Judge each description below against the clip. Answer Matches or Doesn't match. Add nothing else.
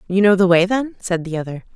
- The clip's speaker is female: Matches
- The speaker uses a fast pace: Matches